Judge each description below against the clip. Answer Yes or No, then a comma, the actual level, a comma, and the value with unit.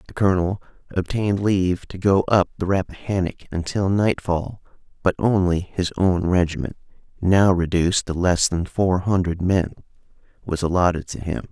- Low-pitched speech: Yes, very low, 90 Hz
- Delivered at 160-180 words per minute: No, average, 145 wpm